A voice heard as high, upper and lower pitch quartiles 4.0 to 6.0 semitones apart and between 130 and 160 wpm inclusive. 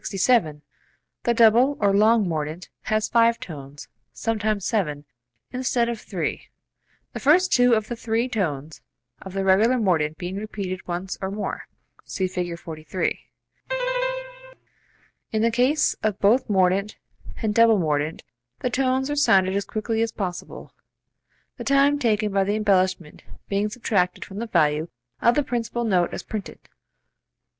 Yes: high, 210 Hz; average, 4.3 semitones; average, 150 wpm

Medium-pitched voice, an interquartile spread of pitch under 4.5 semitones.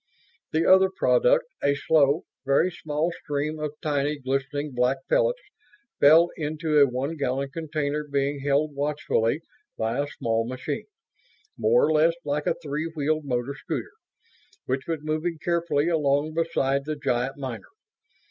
Yes: medium, 145 Hz; narrow, 2.4 semitones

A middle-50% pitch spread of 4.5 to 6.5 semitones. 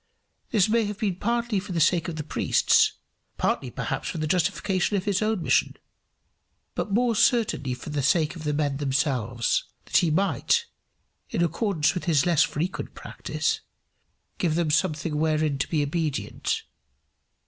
Yes: average, 5.0 semitones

